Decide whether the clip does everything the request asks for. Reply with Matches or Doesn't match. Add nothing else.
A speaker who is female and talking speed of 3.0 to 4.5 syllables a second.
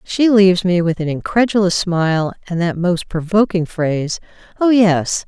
Doesn't match